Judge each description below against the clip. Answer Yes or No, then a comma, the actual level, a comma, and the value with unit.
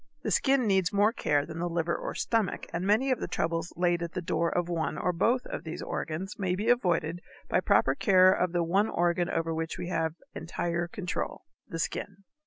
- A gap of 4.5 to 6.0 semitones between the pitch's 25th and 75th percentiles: No, average, 2.7 semitones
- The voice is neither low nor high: Yes, medium, 175 Hz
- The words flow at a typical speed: No, fast, 210 wpm